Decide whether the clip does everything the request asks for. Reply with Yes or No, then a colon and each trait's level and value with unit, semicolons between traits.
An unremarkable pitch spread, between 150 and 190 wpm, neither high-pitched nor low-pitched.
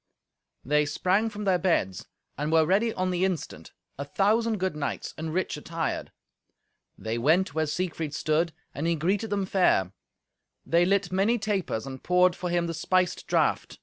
Yes: average, 3.8 semitones; average, 170 wpm; medium, 175 Hz